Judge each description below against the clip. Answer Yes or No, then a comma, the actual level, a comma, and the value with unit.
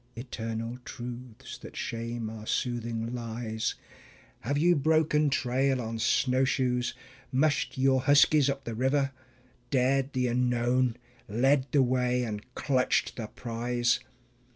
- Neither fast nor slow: No, slow, 120 wpm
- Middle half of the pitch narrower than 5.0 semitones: Yes, narrow, 2.4 semitones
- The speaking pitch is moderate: No, low, 125 Hz